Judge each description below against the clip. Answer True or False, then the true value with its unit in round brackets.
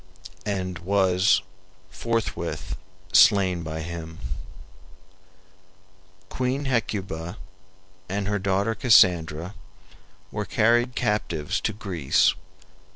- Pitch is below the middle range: True (95 Hz)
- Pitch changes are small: False (4.1 semitones)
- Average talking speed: False (85 wpm)